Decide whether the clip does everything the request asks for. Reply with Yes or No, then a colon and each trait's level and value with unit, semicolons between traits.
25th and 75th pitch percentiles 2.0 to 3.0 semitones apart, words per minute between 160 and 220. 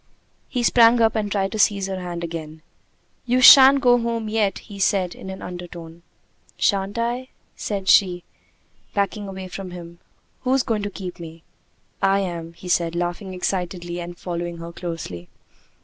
No: average, 3.5 semitones; average, 165 wpm